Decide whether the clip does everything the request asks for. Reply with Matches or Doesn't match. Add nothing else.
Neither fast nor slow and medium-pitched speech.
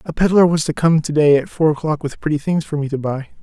Doesn't match